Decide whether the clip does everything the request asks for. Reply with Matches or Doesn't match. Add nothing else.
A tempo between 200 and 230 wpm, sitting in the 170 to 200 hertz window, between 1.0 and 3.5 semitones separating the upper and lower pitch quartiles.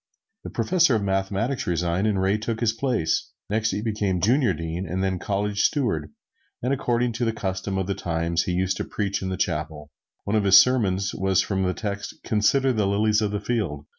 Doesn't match